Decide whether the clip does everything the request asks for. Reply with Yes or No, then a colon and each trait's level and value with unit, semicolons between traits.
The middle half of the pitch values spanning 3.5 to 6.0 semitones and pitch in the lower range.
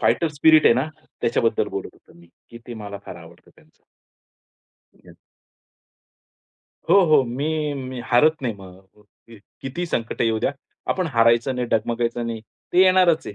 Yes: wide, 5.4 semitones; low, 120 Hz